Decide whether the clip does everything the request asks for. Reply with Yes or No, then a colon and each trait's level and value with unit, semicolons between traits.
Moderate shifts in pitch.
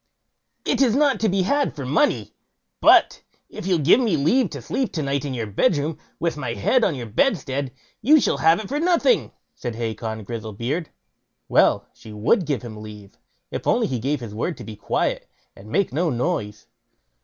No: wide, 8.9 semitones